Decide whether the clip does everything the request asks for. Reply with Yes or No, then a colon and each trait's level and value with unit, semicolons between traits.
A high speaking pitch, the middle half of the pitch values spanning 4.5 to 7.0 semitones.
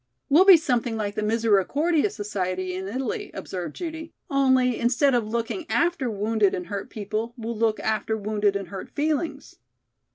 Yes: high, 225 Hz; average, 5.1 semitones